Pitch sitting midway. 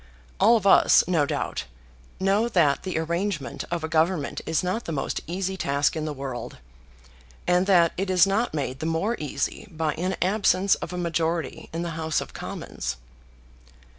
Yes: medium, 170 Hz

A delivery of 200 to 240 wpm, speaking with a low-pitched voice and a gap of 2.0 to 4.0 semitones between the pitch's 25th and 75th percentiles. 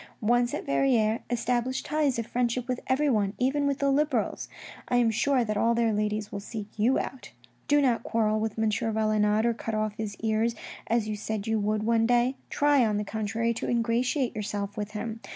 No: fast, 205 wpm; high, 225 Hz; narrow, 2.5 semitones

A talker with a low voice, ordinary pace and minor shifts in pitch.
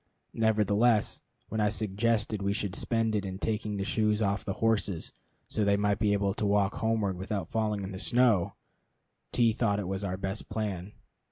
Yes: low, 105 Hz; average, 180 wpm; narrow, 1.9 semitones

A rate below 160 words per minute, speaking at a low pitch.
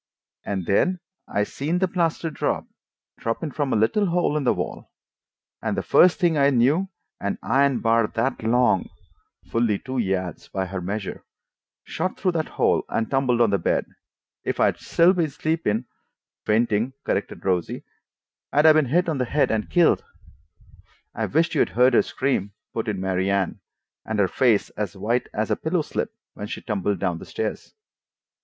No: average, 175 wpm; low, 120 Hz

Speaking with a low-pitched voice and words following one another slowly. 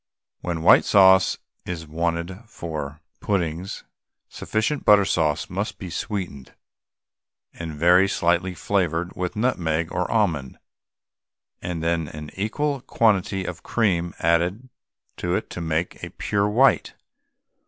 Yes: very low, 90 Hz; slow, 125 wpm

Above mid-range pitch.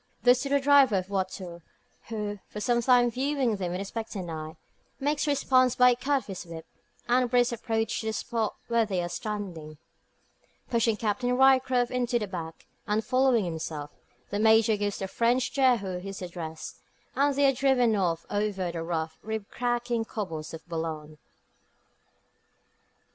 Yes: high, 220 Hz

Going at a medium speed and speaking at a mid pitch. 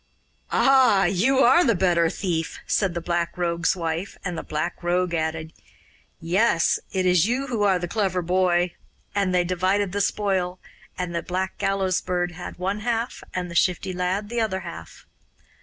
Yes: average, 175 wpm; medium, 180 Hz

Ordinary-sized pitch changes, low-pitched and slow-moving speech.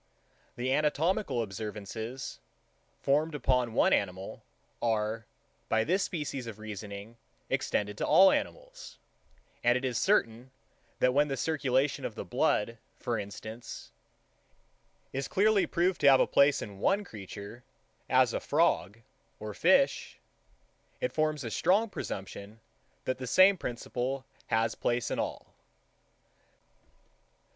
No: wide, 5.8 semitones; low, 125 Hz; slow, 125 wpm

